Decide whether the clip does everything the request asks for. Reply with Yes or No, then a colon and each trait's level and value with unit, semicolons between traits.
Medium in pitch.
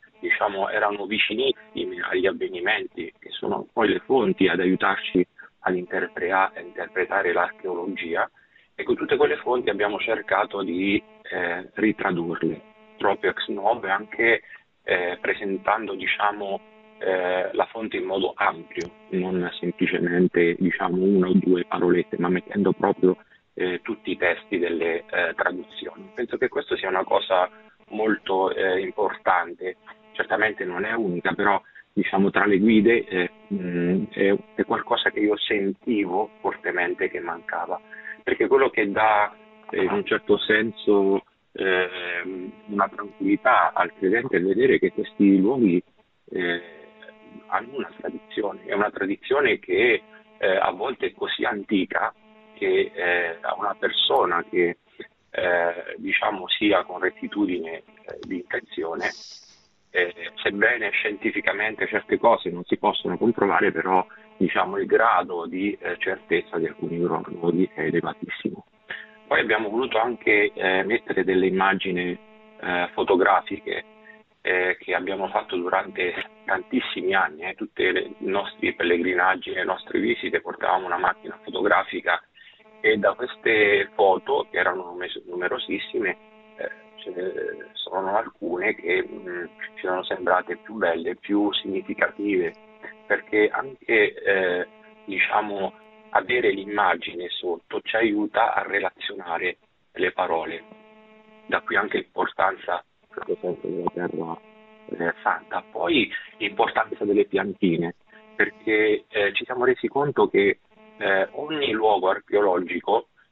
No: high, 215 Hz